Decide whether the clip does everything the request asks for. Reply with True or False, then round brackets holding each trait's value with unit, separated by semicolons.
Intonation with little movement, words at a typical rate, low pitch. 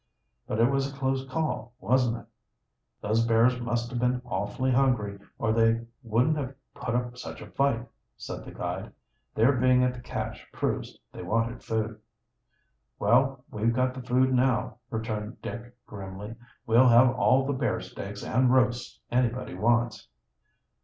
True (2.2 semitones; 160 wpm; 120 Hz)